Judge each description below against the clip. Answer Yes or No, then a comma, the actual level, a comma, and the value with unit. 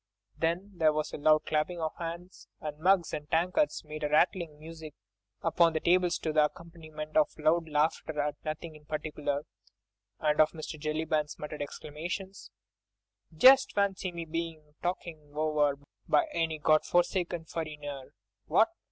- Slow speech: No, average, 145 wpm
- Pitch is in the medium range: Yes, medium, 155 Hz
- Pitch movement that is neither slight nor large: No, narrow, 1.9 semitones